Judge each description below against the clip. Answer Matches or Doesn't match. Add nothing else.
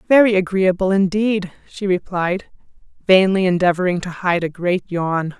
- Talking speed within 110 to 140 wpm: Matches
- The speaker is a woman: Matches